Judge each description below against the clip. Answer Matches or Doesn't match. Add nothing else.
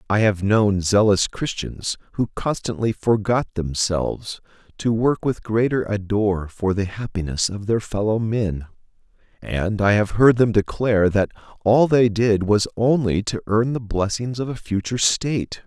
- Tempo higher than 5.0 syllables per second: Doesn't match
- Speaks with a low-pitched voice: Matches